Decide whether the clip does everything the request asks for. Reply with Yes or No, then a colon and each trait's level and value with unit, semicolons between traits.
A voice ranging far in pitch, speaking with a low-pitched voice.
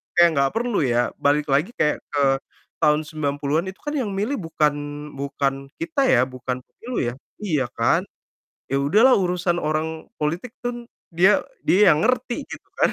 No: wide, 7.6 semitones; medium, 165 Hz